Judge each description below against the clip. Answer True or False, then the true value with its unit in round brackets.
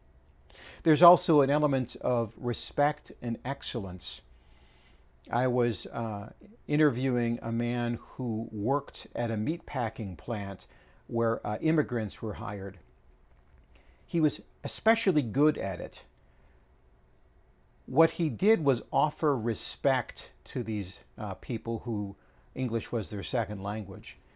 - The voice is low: True (115 Hz)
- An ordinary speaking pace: False (115 wpm)